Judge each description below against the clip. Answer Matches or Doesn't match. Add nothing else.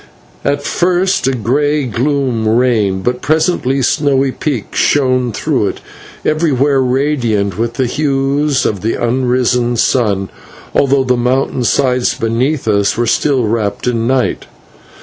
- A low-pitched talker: Matches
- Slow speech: Matches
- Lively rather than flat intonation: Doesn't match